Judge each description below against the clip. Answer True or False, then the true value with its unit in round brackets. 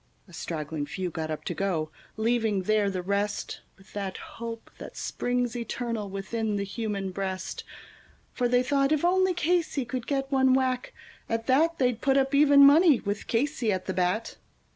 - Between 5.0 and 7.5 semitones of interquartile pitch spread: True (5.5 semitones)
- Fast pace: False (175 wpm)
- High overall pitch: True (230 Hz)